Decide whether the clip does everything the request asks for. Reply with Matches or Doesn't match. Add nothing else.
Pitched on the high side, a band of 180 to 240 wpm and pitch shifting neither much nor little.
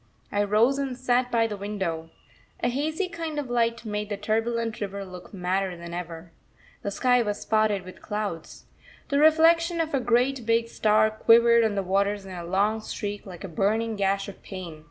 Matches